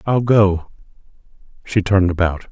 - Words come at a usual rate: No, slow, 120 wpm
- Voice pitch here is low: Yes, very low, 95 Hz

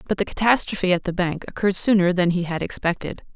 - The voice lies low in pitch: No, medium, 185 Hz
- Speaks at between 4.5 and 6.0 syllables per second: No, 6.6 syllables/s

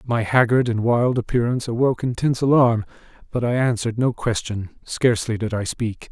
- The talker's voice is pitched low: Yes, low, 115 Hz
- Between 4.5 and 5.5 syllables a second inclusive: No, 5.7 syllables/s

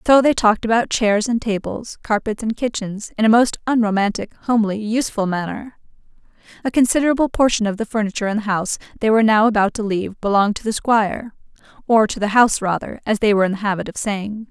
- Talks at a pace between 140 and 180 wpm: No, average, 200 wpm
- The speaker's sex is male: No, female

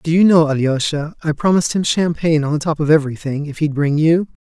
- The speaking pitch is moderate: Yes, medium, 155 Hz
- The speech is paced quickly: Yes, fast, 230 wpm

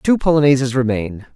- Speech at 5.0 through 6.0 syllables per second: Yes, 5.6 syllables/s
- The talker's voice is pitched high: No, low, 135 Hz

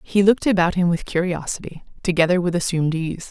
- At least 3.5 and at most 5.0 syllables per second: No, 6.3 syllables/s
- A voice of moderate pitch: Yes, medium, 175 Hz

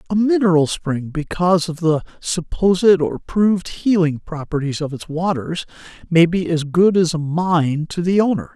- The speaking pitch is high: No, medium, 170 Hz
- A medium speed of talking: Yes, average, 170 wpm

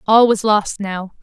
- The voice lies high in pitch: Yes, high, 205 Hz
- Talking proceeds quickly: No, average, 195 wpm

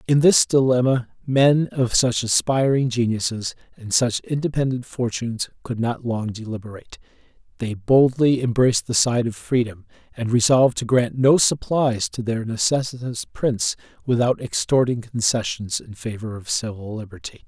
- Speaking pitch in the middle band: No, low, 120 Hz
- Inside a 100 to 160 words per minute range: Yes, average, 140 wpm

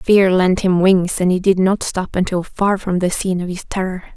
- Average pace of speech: No, fast, 245 wpm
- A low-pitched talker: No, medium, 185 Hz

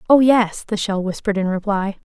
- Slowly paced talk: No, average, 200 wpm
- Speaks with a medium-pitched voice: No, high, 205 Hz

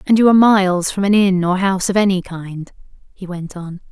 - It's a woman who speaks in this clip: Yes, female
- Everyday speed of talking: No, fast, 230 wpm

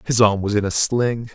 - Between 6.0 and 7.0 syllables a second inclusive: No, 4.9 syllables/s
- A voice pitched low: Yes, low, 110 Hz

